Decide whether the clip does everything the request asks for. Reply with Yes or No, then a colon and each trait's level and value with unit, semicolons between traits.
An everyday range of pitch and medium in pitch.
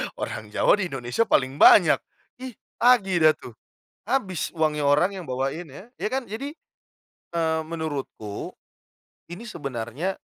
No: wide, 6.6 semitones; medium, 160 Hz